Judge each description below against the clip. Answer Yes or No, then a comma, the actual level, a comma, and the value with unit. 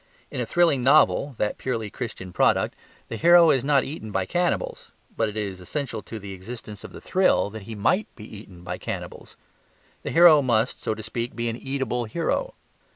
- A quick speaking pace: No, average, 195 wpm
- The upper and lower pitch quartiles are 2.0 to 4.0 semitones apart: No, average, 5.1 semitones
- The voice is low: Yes, low, 115 Hz